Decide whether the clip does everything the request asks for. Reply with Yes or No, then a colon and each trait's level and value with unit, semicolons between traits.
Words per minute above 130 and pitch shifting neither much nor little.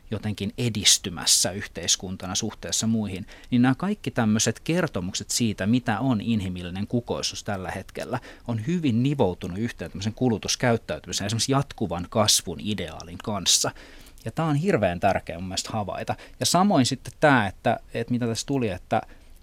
Yes: average, 140 wpm; average, 4.5 semitones